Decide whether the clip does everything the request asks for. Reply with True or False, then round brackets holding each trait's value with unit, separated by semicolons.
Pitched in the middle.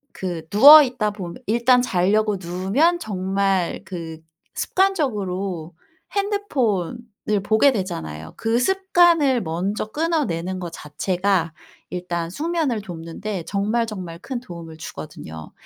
False (200 Hz)